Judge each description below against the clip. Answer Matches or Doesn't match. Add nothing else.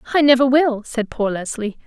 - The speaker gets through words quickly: Doesn't match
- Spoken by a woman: Matches